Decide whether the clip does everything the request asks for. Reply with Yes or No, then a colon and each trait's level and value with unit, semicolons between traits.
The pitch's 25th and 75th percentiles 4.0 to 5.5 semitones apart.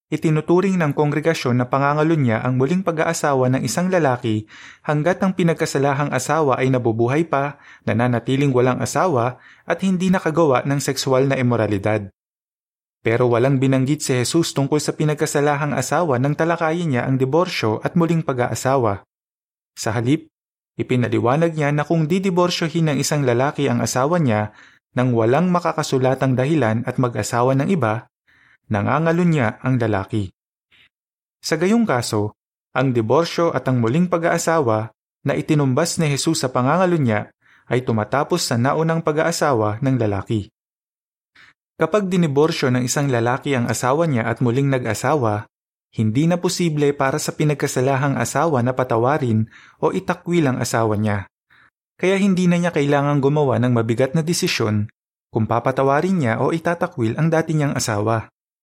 Yes: average, 5.2 semitones